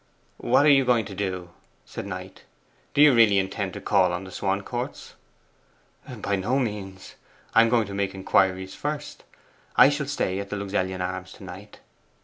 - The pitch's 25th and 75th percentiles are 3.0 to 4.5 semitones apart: Yes, average, 4.1 semitones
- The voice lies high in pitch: No, low, 100 Hz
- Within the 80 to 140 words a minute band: No, average, 175 wpm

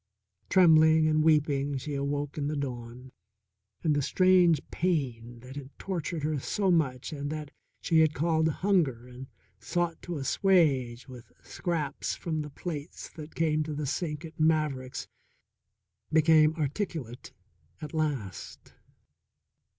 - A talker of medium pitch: Yes, medium, 150 Hz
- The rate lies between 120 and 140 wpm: Yes, slow, 135 wpm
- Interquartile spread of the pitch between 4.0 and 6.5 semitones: No, average, 2.9 semitones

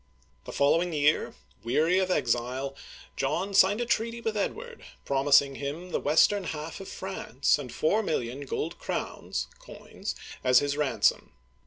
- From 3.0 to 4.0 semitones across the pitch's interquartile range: No, wide, 5.6 semitones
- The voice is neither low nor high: Yes, medium, 150 Hz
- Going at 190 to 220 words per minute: No, average, 145 wpm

